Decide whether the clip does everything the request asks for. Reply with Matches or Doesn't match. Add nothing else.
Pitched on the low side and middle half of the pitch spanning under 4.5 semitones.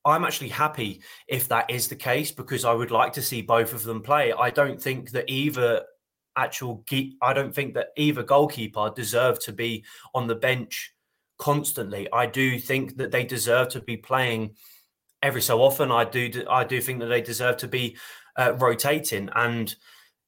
Matches